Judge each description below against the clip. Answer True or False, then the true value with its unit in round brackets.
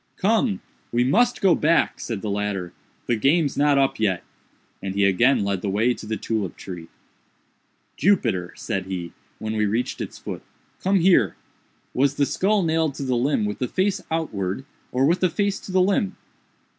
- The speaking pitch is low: True (130 Hz)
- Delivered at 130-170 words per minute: False (180 wpm)